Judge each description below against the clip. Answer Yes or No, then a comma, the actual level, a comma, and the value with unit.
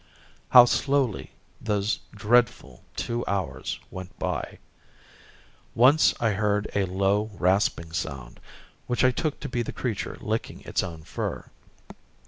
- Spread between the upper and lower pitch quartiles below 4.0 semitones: No, average, 4.6 semitones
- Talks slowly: Yes, slow, 125 wpm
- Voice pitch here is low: Yes, low, 105 Hz